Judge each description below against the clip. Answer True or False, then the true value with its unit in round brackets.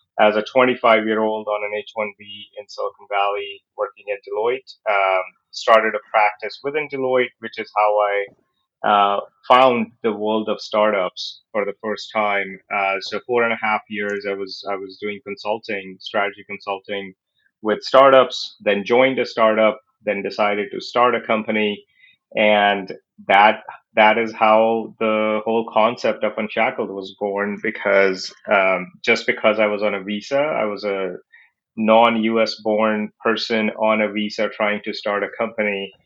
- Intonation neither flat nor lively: False (2.0 semitones)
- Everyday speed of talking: True (165 wpm)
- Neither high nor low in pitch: False (105 Hz)